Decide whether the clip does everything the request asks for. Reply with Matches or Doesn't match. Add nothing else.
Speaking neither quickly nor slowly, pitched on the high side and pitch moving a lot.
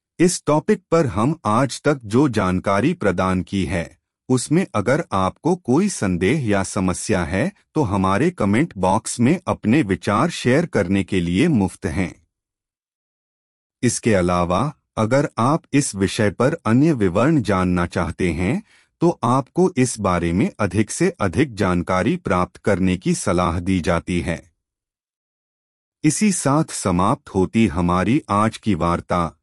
Doesn't match